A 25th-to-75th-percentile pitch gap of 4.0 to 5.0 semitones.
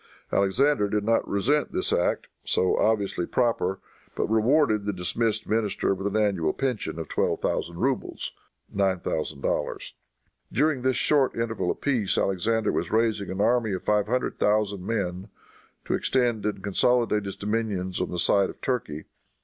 No: average, 3.3 semitones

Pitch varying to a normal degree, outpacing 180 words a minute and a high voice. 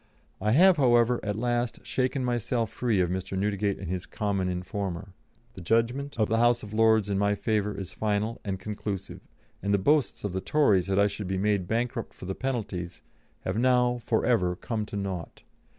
No: average, 3.7 semitones; average, 195 wpm; low, 105 Hz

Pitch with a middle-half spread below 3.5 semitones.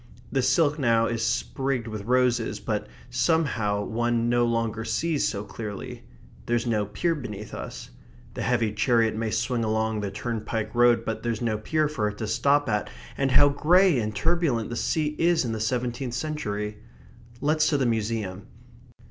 No: average, 3.9 semitones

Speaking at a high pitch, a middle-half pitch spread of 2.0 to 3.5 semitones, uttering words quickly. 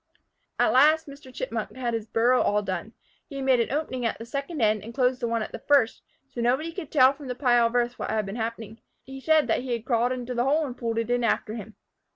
Yes: high, 245 Hz; average, 2.8 semitones; fast, 255 wpm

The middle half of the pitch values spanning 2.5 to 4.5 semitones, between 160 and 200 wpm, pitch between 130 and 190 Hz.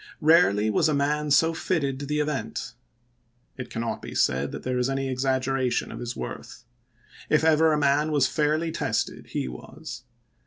Yes: average, 3.0 semitones; average, 170 wpm; medium, 140 Hz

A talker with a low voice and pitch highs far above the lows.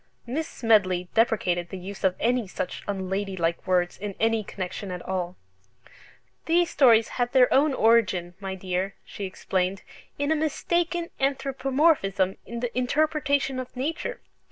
No: high, 225 Hz; wide, 6.4 semitones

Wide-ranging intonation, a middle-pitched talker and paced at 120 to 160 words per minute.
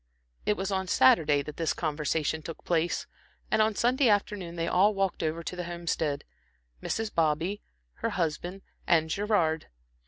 No: average, 3.6 semitones; medium, 170 Hz; average, 155 wpm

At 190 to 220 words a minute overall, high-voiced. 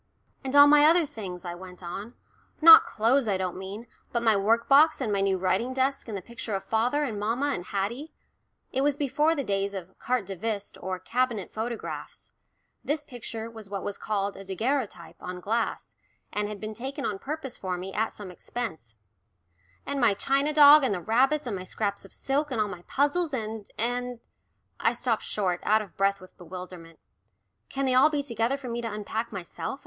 Yes: average, 200 wpm; high, 225 Hz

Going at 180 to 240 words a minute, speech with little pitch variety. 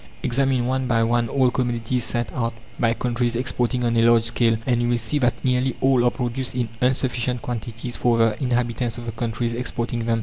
Yes: fast, 205 wpm; narrow, 1.3 semitones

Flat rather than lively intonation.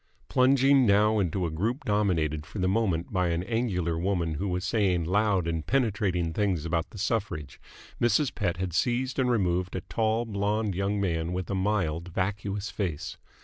No: average, 3.7 semitones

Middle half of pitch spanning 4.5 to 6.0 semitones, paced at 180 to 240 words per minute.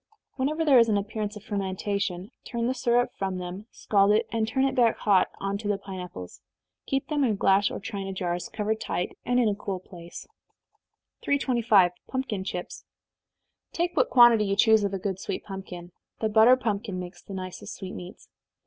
No: average, 3.7 semitones; average, 185 wpm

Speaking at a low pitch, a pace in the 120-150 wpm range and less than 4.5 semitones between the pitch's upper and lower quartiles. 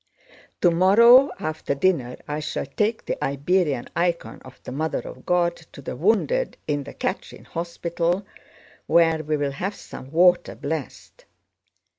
No: medium, 165 Hz; average, 140 wpm; average, 3.9 semitones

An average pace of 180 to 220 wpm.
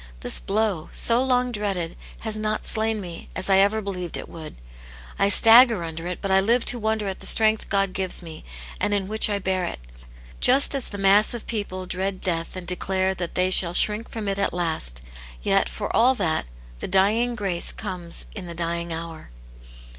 Yes: average, 200 wpm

